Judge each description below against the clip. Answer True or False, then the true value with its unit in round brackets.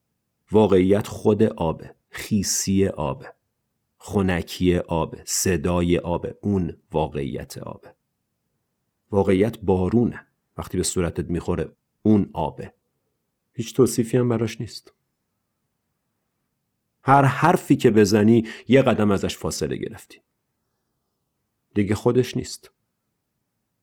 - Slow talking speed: True (95 wpm)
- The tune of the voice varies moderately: True (4.6 semitones)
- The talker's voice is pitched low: True (100 Hz)